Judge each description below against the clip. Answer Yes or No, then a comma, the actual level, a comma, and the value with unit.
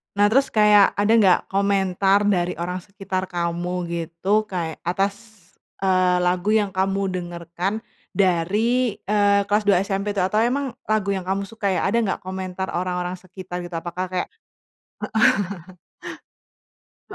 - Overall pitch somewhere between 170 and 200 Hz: Yes, high, 190 Hz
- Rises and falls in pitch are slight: Yes, narrow, 2.2 semitones